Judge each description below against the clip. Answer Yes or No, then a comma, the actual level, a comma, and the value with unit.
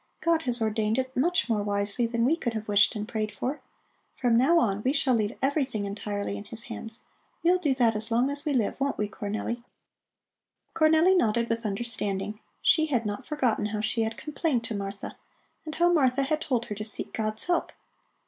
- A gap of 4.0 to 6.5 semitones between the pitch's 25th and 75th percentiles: Yes, average, 4.6 semitones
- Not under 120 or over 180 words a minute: No, average, 200 wpm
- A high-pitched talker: Yes, high, 235 Hz